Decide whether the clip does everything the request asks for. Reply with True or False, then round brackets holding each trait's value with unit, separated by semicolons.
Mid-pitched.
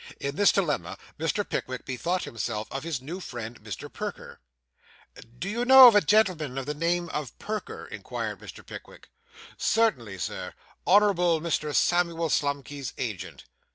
True (160 Hz)